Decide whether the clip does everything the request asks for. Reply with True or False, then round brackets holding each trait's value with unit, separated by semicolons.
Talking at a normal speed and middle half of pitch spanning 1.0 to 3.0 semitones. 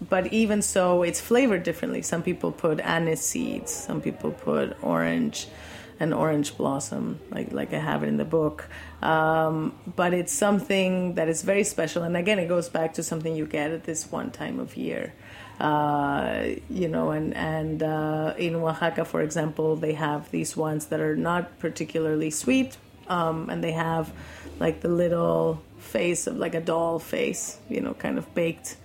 True (180 wpm; 2.4 semitones)